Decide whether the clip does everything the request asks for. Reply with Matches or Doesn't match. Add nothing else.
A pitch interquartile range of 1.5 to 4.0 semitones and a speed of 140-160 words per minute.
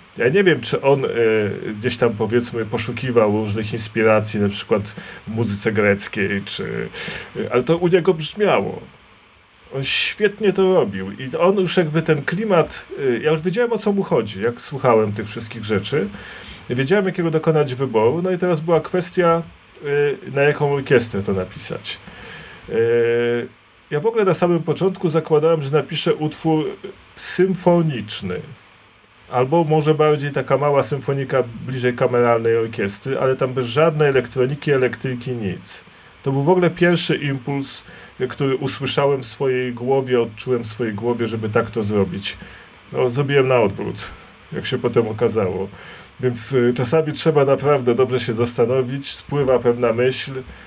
Doesn't match